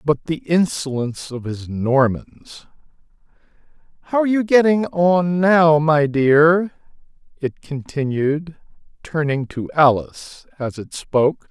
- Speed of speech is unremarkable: No, slow, 115 wpm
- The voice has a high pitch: No, medium, 150 Hz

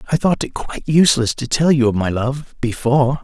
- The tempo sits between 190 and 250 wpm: Yes, fast, 205 wpm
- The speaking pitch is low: Yes, low, 130 Hz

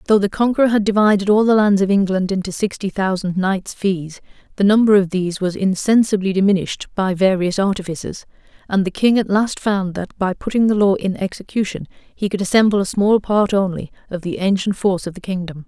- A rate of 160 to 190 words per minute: No, average, 200 wpm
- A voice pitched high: Yes, high, 195 Hz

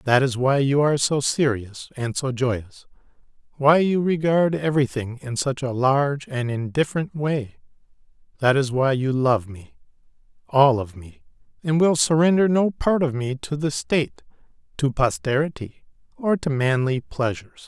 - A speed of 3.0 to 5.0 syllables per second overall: Yes, 4.7 syllables/s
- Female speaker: No, male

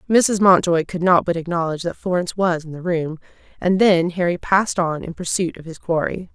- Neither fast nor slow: No, fast, 210 wpm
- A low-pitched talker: No, medium, 175 Hz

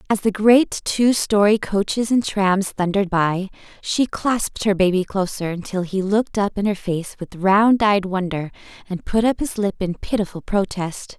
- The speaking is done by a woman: Yes, female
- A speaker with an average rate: Yes, average, 180 wpm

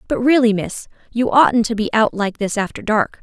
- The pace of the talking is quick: Yes, fast, 225 wpm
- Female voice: Yes, female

